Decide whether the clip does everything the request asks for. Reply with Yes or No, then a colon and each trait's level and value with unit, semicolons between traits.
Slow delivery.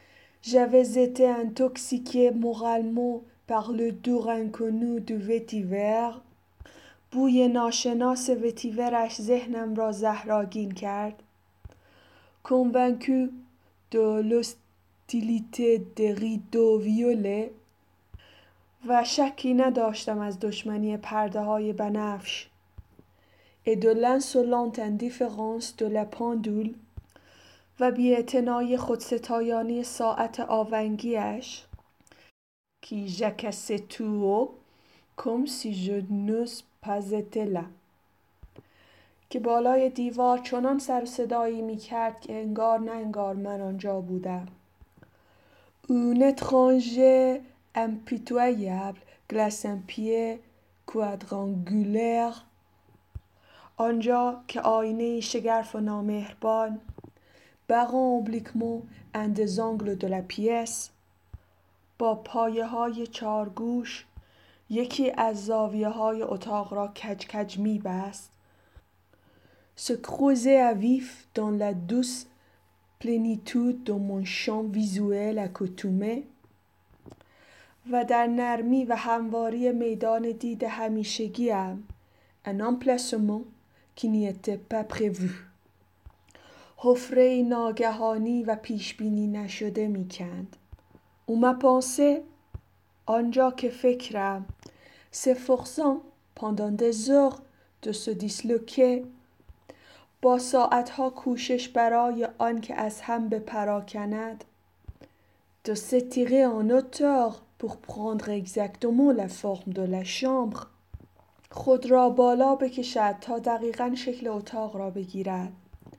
Yes: slow, 85 wpm